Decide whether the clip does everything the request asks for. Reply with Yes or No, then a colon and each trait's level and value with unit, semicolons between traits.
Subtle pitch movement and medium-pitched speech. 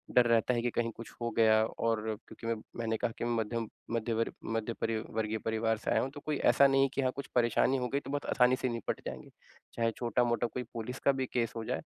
No: narrow, 1.8 semitones; low, 115 Hz